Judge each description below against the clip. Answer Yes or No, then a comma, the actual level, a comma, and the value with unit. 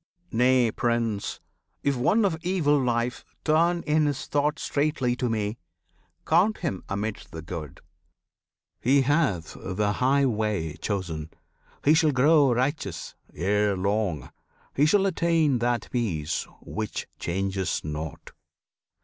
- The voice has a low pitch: Yes, low, 120 Hz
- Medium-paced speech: No, slow, 125 wpm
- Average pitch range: No, wide, 6.9 semitones